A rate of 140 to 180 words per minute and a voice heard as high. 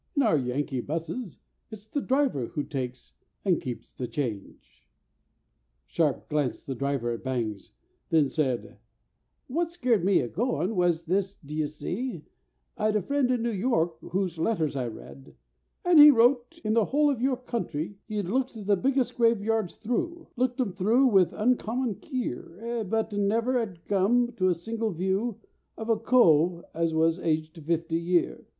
Yes: average, 165 wpm; high, 195 Hz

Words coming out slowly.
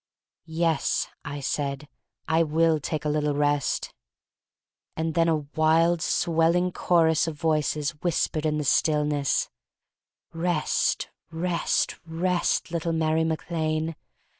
Yes: slow, 115 wpm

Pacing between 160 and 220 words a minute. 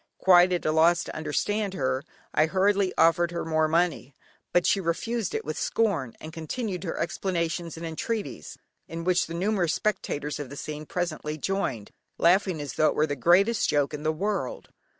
Yes: average, 185 wpm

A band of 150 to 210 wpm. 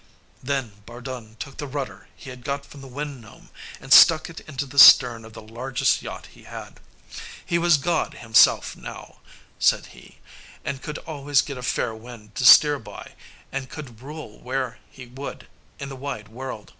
Yes: average, 180 wpm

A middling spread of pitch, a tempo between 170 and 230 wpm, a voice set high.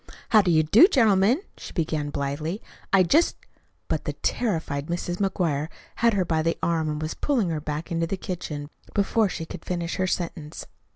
No: average, 4.0 semitones; average, 190 wpm; medium, 170 Hz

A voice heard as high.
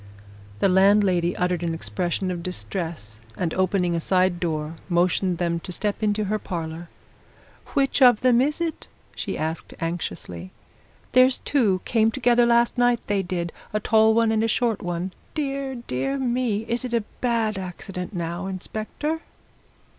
Yes: high, 195 Hz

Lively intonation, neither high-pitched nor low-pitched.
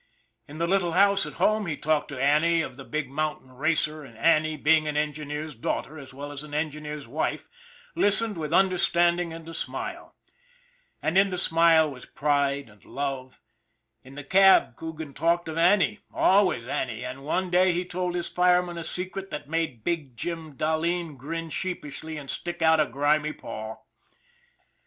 No: average, 3.2 semitones; medium, 155 Hz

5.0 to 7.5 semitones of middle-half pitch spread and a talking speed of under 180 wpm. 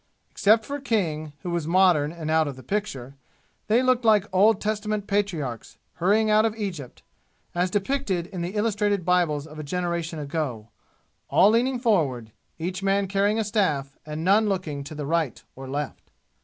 Yes: wide, 5.4 semitones; average, 170 wpm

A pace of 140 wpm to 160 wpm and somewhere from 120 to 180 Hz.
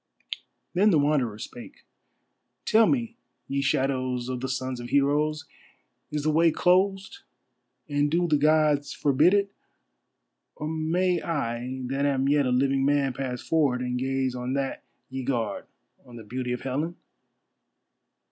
Yes: average, 145 wpm; medium, 140 Hz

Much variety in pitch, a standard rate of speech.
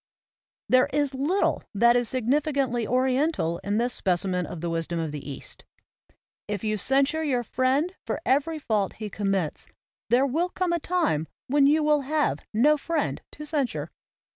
Yes: wide, 6.3 semitones; average, 165 wpm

